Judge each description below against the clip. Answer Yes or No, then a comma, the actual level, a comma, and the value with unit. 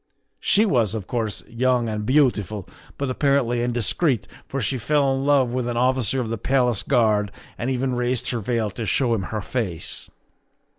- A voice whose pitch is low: Yes, low, 120 Hz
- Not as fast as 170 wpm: No, average, 180 wpm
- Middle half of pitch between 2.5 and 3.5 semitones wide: Yes, average, 3.0 semitones